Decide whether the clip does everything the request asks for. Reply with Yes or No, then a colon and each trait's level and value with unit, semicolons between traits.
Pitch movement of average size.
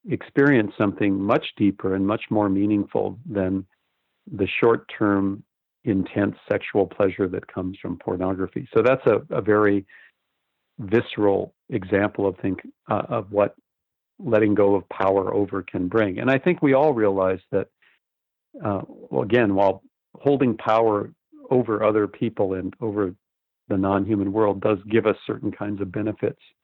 No: narrow, 1.9 semitones